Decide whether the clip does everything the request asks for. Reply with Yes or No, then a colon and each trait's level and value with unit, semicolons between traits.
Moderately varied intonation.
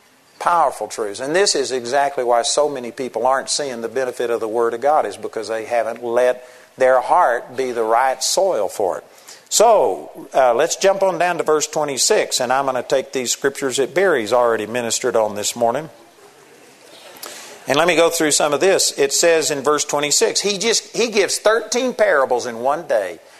No: wide, 6.2 semitones